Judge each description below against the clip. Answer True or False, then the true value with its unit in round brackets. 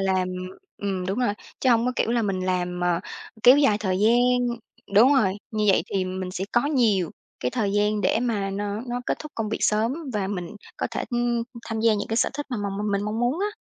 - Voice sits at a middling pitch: False (210 Hz)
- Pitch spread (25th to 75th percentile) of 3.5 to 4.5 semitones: True (3.8 semitones)